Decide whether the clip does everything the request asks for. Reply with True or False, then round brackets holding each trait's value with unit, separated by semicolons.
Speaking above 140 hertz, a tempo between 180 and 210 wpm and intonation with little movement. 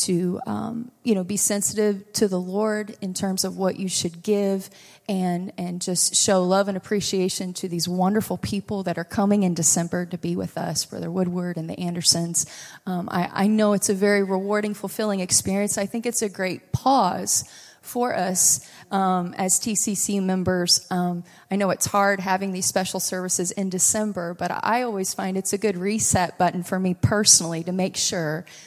True (190 Hz; 185 wpm; 2.2 semitones)